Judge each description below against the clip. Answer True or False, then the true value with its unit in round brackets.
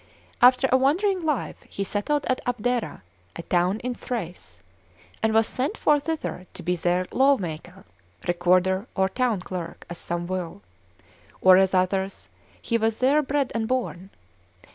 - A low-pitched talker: False (205 Hz)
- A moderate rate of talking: True (150 wpm)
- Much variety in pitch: True (6.0 semitones)